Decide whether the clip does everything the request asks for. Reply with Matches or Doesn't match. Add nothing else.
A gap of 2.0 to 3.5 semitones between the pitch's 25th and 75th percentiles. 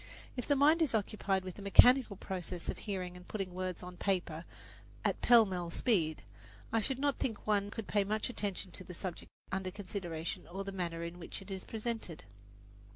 Matches